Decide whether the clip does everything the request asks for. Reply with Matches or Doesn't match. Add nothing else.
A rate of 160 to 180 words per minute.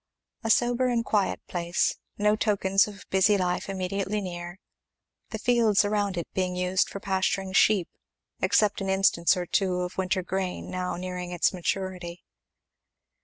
Doesn't match